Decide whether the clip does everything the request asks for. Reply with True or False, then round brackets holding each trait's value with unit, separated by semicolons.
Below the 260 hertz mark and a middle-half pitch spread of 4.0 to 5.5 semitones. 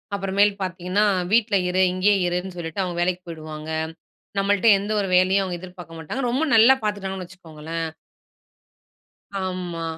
False (185 Hz; 2.5 semitones)